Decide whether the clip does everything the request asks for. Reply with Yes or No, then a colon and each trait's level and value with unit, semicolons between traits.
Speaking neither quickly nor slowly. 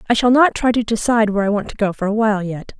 No: fast, 320 wpm